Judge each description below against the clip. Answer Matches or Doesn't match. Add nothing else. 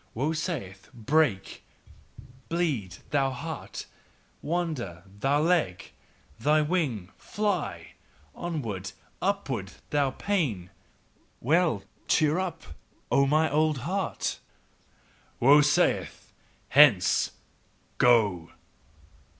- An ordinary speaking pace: Doesn't match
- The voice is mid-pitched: Matches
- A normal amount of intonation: Doesn't match